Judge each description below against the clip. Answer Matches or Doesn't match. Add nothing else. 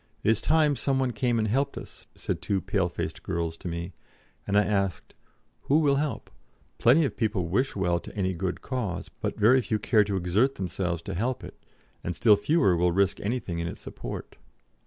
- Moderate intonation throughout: Doesn't match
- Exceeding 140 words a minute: Matches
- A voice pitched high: Doesn't match